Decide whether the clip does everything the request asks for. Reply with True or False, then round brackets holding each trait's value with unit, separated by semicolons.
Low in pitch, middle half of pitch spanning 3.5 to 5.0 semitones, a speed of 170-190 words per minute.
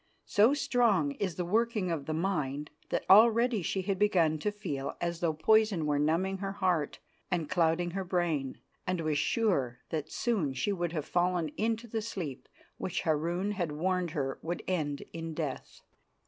False (175 Hz; 4.4 semitones; 175 wpm)